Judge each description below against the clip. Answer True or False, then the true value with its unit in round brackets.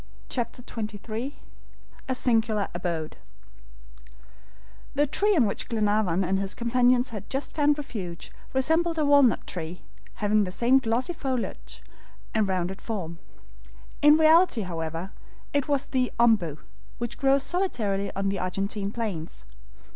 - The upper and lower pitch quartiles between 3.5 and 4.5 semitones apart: False (5.6 semitones)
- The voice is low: False (225 Hz)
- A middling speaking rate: False (130 wpm)